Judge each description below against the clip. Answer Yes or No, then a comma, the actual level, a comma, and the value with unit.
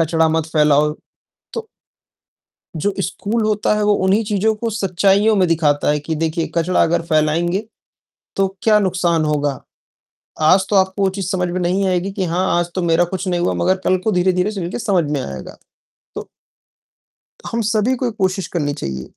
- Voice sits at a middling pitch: Yes, medium, 180 Hz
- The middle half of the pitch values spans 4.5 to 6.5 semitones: No, average, 3.5 semitones